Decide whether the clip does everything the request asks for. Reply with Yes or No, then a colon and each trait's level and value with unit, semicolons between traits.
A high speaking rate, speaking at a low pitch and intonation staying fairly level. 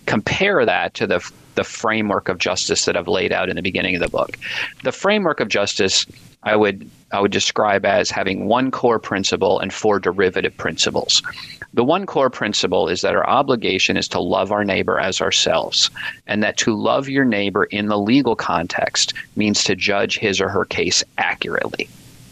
No: average, 185 wpm; low, 105 Hz; narrow, 1.0 semitones